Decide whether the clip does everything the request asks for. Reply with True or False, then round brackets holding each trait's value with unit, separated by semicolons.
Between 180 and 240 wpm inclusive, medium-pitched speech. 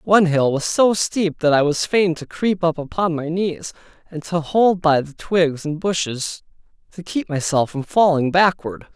True (195 wpm; 165 Hz)